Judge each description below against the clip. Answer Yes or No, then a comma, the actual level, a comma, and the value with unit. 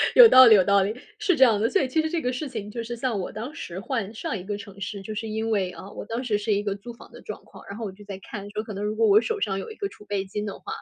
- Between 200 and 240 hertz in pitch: Yes, high, 215 Hz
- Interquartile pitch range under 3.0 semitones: No, average, 3.3 semitones